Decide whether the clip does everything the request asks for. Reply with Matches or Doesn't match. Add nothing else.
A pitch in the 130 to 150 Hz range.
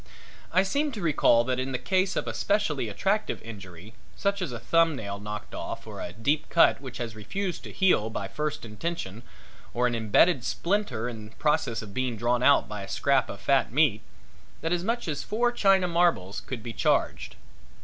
Matches